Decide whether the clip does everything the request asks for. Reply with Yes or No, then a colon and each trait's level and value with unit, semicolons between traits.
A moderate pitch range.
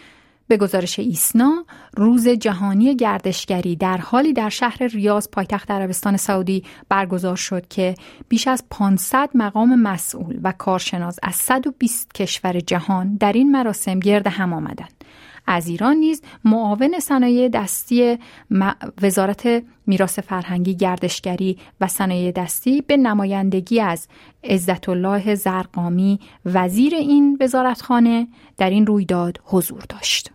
Yes: average, 4.5 semitones